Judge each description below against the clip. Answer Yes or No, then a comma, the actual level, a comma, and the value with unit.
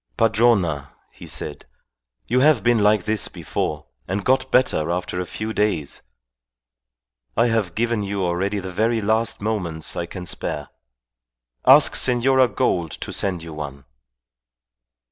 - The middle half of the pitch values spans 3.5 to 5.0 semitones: Yes, average, 4.7 semitones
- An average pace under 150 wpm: Yes, average, 140 wpm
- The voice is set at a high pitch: No, low, 100 Hz